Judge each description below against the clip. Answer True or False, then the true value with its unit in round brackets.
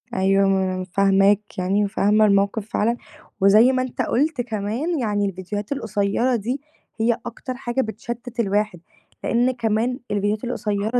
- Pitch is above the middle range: True (215 Hz)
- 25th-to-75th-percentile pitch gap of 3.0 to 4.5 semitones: True (3.3 semitones)